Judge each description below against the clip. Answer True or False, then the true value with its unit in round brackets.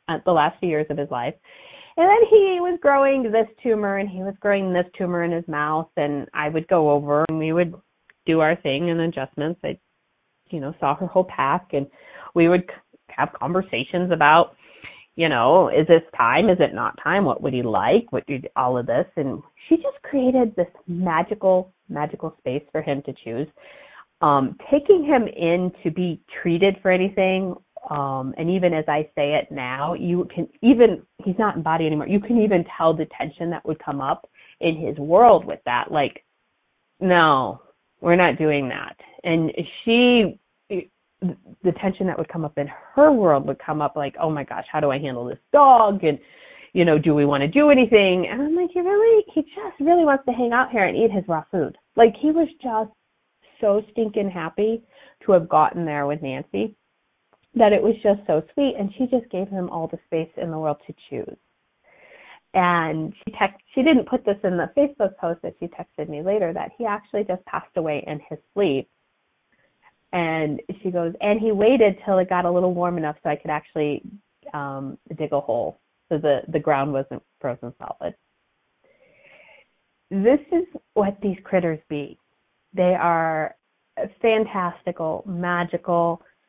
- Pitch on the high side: False (180 Hz)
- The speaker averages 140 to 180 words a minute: False (190 wpm)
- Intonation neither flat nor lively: False (5.7 semitones)